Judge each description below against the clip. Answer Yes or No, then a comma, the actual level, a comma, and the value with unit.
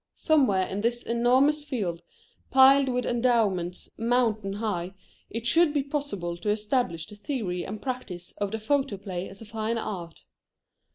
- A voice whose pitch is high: Yes, high, 220 Hz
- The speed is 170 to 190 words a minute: No, average, 150 wpm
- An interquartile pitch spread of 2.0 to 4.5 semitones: No, average, 5.0 semitones